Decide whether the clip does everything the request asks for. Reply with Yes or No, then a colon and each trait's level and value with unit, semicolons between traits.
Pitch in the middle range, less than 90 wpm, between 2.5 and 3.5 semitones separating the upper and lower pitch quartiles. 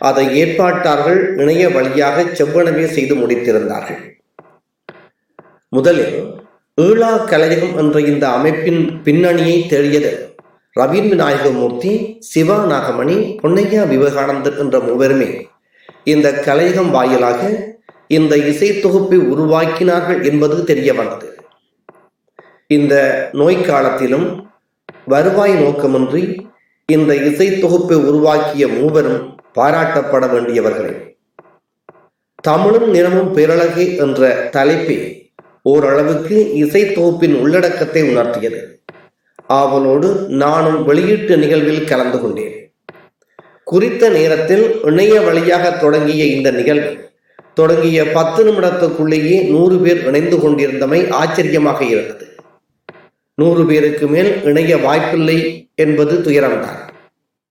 No: medium, 160 Hz; average, 80 wpm; average, 4.1 semitones